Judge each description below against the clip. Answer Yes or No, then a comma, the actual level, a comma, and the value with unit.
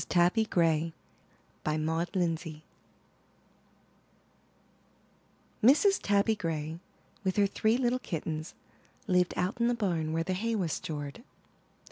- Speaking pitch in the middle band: Yes, medium, 180 Hz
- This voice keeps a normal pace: No, slow, 110 wpm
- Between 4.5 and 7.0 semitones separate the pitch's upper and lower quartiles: Yes, average, 5.1 semitones